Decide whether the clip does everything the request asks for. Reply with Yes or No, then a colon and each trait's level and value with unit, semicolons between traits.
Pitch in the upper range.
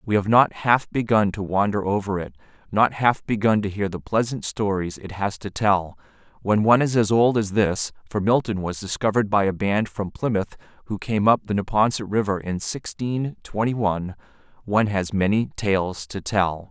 No: low, 105 Hz